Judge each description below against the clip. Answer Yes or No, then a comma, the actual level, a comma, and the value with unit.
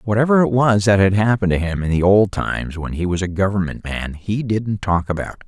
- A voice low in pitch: Yes, low, 100 Hz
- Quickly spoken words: Yes, fast, 240 wpm